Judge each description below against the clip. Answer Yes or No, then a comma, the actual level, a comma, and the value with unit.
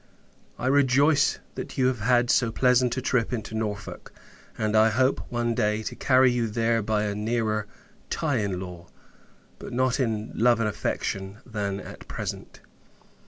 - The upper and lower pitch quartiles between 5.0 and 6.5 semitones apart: No, average, 2.9 semitones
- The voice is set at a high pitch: No, low, 115 Hz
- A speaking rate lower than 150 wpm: No, average, 165 wpm